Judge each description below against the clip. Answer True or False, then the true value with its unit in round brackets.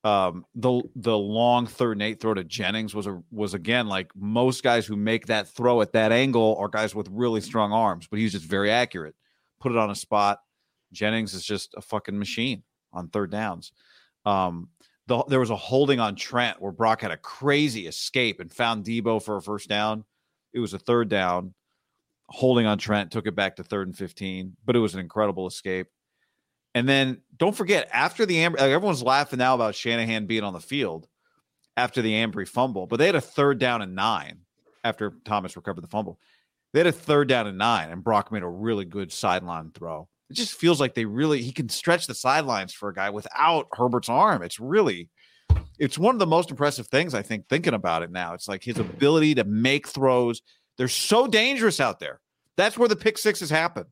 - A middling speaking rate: False (210 wpm)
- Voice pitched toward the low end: True (115 Hz)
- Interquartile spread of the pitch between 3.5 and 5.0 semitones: True (4.2 semitones)